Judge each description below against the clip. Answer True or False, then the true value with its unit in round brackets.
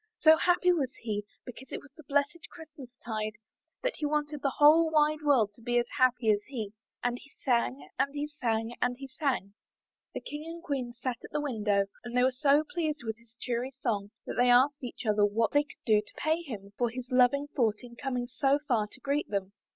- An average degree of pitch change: True (4.2 semitones)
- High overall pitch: True (255 Hz)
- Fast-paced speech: True (220 wpm)